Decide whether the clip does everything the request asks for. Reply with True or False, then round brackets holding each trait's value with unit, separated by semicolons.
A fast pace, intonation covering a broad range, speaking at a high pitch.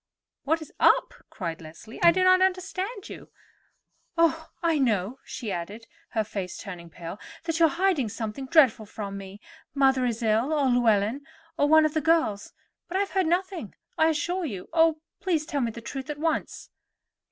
False (185 wpm; 7.4 semitones; 280 Hz)